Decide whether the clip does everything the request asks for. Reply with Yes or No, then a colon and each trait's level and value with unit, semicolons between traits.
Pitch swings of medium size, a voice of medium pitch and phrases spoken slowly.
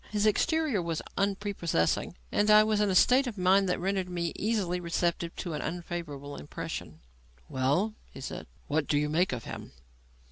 No: average, 4.1 semitones; medium, 180 Hz; average, 175 wpm